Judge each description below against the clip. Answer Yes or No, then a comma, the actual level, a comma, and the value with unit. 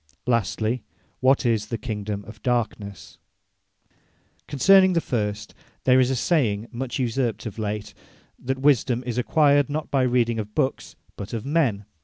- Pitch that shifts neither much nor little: Yes, average, 3.6 semitones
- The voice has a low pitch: Yes, low, 120 Hz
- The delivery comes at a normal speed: Yes, average, 150 wpm